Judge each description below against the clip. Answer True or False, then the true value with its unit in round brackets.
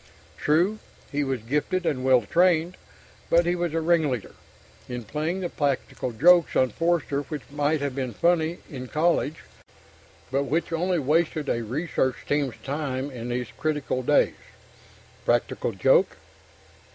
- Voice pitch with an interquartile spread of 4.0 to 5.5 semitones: True (4.4 semitones)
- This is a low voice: False (150 Hz)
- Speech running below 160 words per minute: True (140 wpm)